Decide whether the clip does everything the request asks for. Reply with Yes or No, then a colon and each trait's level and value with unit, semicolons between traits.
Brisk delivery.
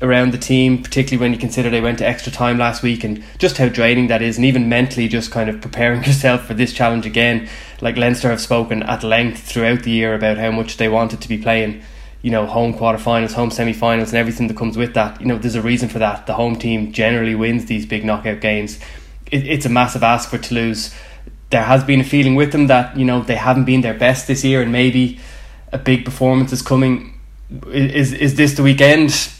Yes: fast, 230 wpm